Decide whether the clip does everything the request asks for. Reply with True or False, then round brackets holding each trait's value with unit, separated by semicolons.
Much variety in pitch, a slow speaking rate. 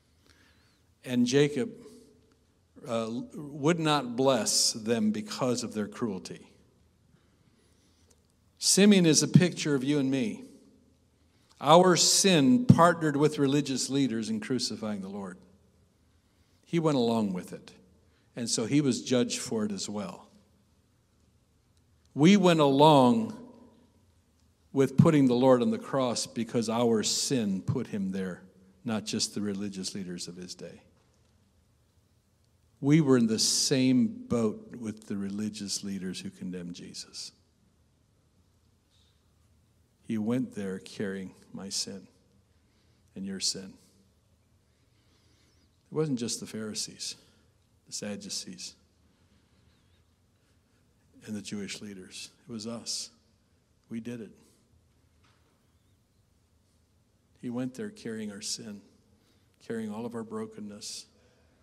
True (6.5 semitones; 115 wpm)